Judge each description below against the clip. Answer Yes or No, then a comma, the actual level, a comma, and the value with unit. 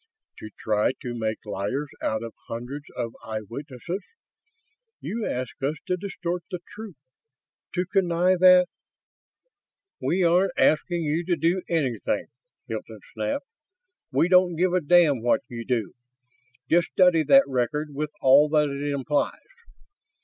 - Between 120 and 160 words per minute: Yes, average, 140 wpm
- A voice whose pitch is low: No, medium, 150 Hz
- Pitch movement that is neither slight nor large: No, wide, 5.9 semitones